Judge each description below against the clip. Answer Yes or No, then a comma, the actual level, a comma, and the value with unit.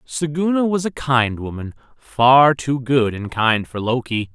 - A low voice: Yes, low, 130 Hz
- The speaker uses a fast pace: No, average, 165 wpm